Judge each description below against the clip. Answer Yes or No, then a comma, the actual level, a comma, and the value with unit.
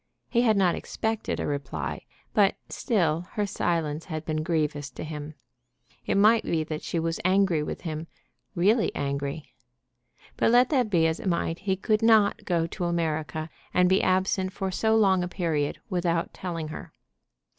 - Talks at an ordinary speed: Yes, average, 170 wpm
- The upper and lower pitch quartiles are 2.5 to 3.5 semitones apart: No, average, 4.0 semitones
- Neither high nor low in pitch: Yes, medium, 175 Hz